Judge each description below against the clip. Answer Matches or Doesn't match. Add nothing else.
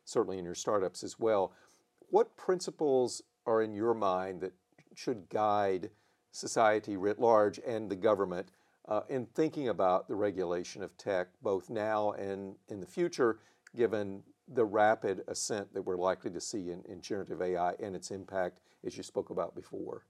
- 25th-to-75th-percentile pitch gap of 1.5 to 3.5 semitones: Matches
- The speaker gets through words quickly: Doesn't match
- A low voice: Matches